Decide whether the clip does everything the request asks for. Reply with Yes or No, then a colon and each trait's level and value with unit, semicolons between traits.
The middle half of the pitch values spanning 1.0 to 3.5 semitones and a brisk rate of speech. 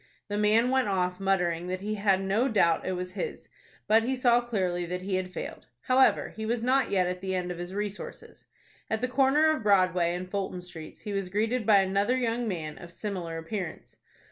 No: average, 3.9 semitones; fast, 210 wpm